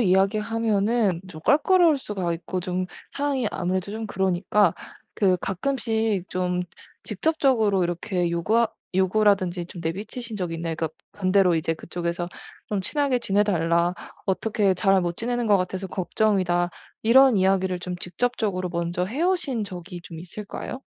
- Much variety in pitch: No, average, 3.9 semitones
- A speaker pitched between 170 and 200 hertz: Yes, high, 190 Hz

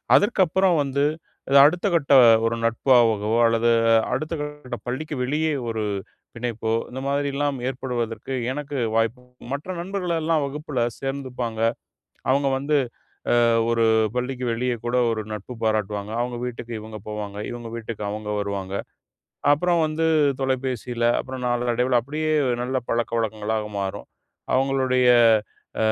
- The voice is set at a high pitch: No, low, 125 Hz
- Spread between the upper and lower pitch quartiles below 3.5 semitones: No, average, 4.0 semitones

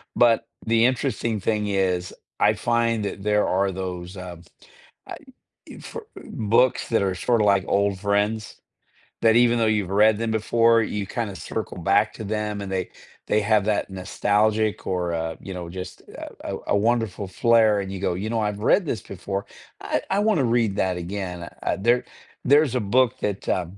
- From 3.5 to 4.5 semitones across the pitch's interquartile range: No, average, 3.1 semitones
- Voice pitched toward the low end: Yes, low, 105 Hz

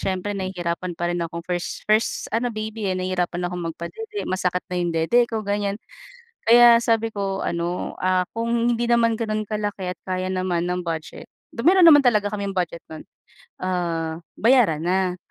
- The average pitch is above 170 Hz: Yes, high, 190 Hz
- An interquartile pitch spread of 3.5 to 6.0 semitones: Yes, average, 4.2 semitones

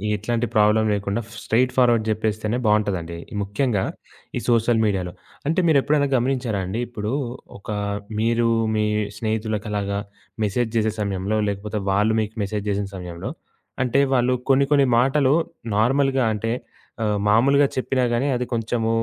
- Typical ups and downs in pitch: Yes, average, 3.2 semitones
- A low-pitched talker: Yes, low, 110 Hz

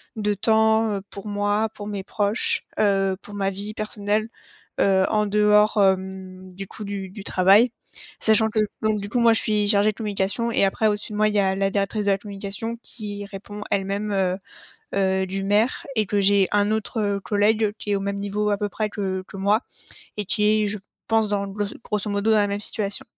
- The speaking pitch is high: Yes, high, 205 Hz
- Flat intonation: Yes, narrow, 1.4 semitones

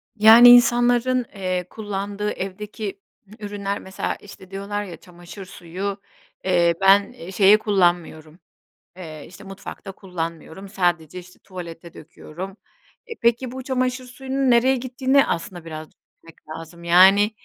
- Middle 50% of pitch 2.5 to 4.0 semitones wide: No, average, 4.6 semitones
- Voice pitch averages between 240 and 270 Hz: No, high, 195 Hz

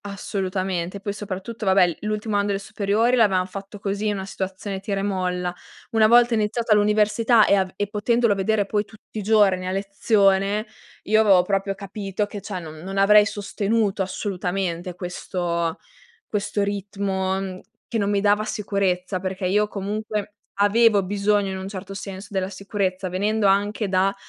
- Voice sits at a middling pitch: No, high, 200 Hz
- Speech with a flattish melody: Yes, narrow, 1.7 semitones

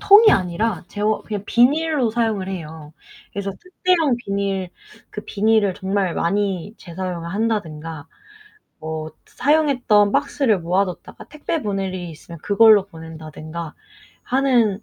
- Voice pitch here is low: No, high, 200 Hz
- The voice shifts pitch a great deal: No, average, 4.9 semitones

